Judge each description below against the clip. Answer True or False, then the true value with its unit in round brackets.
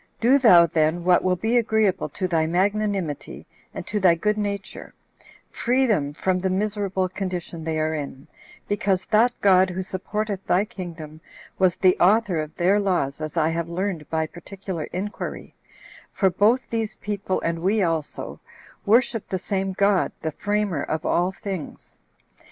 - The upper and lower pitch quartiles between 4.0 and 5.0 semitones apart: False (3.6 semitones)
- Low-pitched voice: False (185 Hz)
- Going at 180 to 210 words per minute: False (160 wpm)